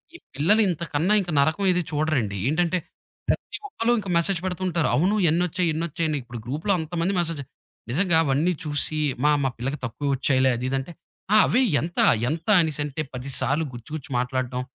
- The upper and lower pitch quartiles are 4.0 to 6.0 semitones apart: Yes, average, 4.4 semitones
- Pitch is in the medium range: Yes, medium, 155 Hz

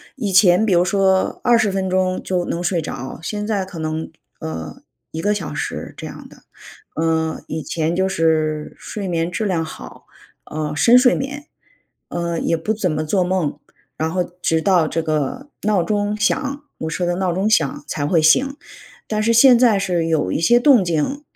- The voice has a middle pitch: Yes, medium, 180 Hz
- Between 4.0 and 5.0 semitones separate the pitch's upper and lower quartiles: Yes, average, 4.6 semitones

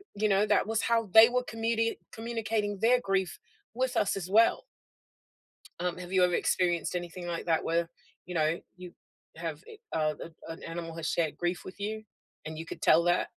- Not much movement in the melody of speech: No, average, 4.6 semitones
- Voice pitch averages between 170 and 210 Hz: Yes, medium, 185 Hz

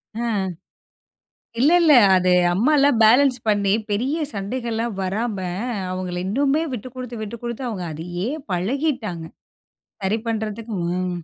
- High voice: Yes, high, 225 Hz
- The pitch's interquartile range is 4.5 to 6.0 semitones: Yes, average, 5.0 semitones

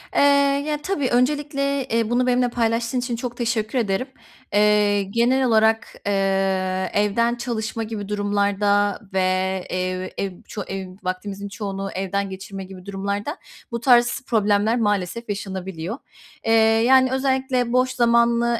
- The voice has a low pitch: No, high, 220 Hz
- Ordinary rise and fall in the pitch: Yes, average, 3.8 semitones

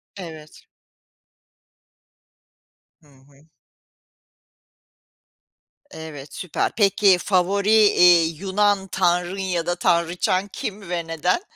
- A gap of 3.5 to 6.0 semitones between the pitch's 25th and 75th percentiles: No, average, 3.0 semitones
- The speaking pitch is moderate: Yes, medium, 180 Hz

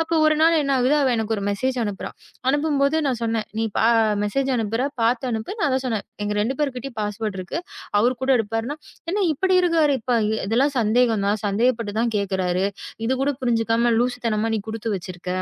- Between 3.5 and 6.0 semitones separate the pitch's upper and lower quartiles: Yes, average, 4.2 semitones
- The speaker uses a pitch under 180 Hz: No, high, 230 Hz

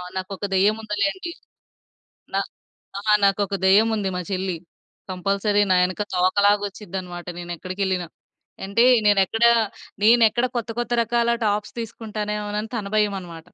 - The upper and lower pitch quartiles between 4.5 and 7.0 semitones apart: No, narrow, 2.5 semitones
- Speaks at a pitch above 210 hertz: No, high, 205 Hz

